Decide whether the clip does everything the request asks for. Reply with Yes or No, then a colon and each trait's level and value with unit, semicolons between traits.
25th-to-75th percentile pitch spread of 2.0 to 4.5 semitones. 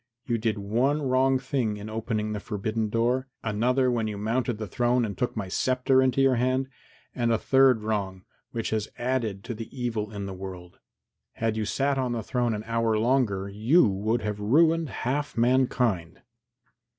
Yes: average, 3.4 semitones